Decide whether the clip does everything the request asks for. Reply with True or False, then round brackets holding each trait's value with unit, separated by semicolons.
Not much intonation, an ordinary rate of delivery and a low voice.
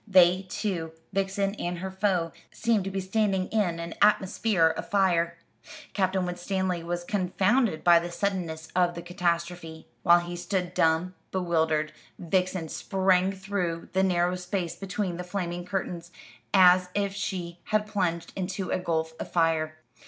False (2.1 semitones; 150 wpm; 180 Hz)